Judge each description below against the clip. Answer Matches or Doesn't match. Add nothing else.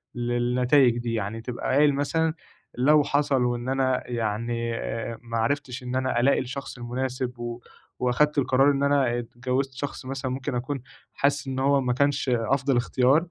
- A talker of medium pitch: Doesn't match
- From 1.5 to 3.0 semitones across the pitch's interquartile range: Matches